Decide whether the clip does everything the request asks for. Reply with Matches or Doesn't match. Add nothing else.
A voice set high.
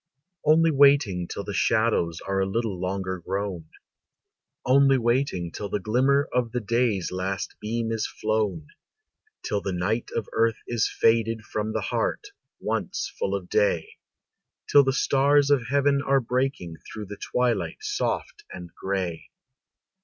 Doesn't match